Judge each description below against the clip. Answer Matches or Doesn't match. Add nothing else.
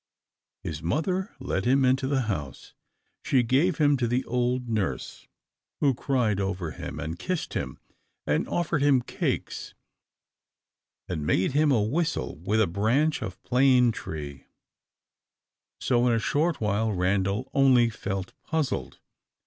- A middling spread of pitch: Doesn't match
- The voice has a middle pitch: Doesn't match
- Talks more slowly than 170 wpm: Matches